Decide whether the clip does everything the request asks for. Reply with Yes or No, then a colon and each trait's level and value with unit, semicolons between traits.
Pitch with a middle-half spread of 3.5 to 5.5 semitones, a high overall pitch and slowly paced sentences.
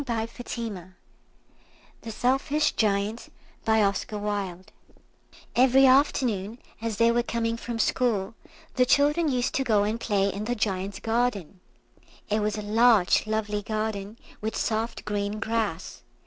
No: average, 2.7 semitones; high, 220 Hz; slow, 120 wpm